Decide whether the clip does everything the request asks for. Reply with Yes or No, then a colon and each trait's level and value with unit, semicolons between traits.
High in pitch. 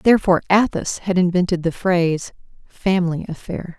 No: medium, 180 Hz